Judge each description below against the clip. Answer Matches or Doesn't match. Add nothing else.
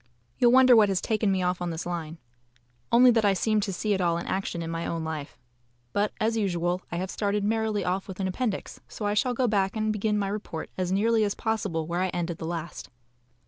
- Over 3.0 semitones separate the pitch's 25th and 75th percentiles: Matches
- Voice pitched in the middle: Doesn't match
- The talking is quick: Matches